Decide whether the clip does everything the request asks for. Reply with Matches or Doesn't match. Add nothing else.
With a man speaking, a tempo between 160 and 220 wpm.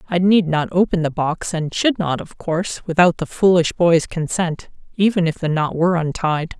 Doesn't match